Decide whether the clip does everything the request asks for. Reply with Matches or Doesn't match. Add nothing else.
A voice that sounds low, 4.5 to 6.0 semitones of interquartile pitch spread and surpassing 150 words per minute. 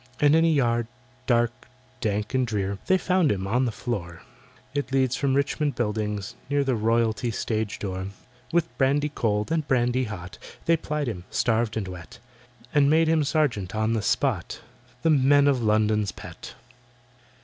Matches